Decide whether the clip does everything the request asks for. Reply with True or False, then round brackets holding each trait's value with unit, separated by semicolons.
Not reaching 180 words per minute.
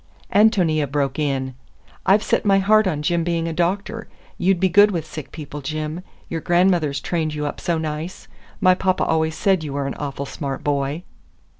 False (185 wpm)